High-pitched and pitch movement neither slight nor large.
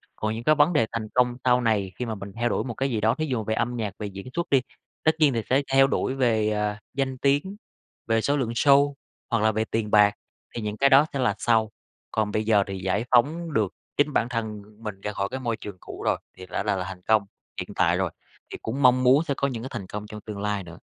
No: low, 115 Hz; average, 4.0 semitones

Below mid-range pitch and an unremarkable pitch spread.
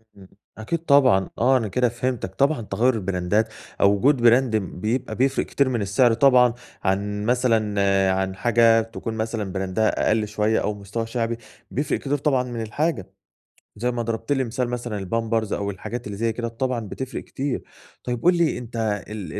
Yes: low, 115 Hz; average, 3.1 semitones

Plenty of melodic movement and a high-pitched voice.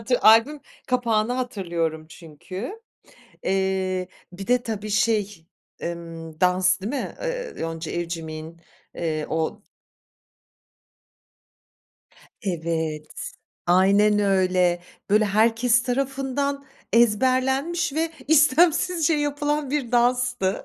Yes: wide, 6.8 semitones; high, 215 Hz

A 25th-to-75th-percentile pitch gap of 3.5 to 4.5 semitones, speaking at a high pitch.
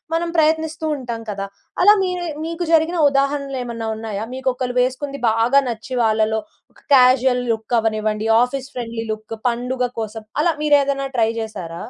Yes: average, 3.9 semitones; very high, 250 Hz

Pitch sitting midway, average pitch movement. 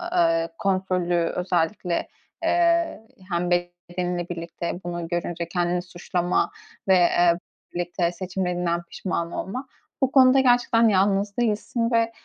Yes: medium, 180 Hz; average, 3.3 semitones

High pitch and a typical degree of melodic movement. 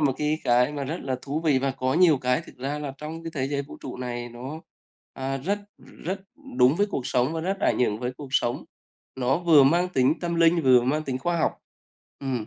No: medium, 140 Hz; average, 4.1 semitones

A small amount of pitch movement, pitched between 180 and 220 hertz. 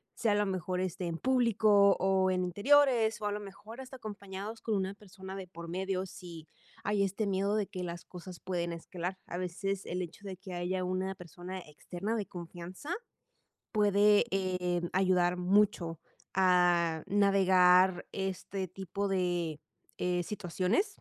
Yes: narrow, 2.2 semitones; high, 190 Hz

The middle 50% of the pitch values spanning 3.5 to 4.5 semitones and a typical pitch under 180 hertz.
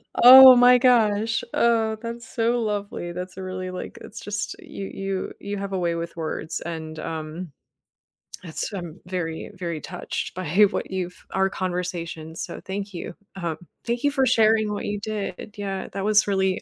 No: average, 3.8 semitones; high, 195 Hz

